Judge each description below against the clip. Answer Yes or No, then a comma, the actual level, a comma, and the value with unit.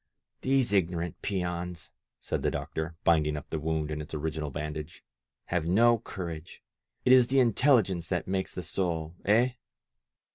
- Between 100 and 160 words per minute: Yes, average, 150 wpm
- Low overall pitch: Yes, very low, 85 Hz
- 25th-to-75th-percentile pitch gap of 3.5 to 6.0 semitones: Yes, average, 4.5 semitones